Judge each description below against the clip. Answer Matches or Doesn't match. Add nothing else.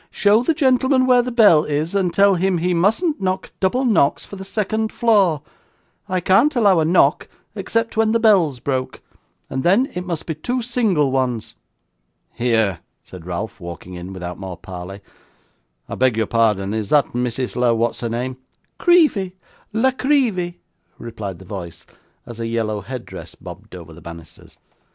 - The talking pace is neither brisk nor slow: Matches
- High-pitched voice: Doesn't match